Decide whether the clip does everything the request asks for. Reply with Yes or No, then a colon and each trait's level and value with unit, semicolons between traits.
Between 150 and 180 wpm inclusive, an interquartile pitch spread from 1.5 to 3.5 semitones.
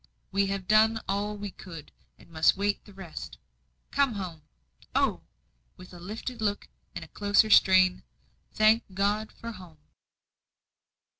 No: average, 140 wpm; average, 2.7 semitones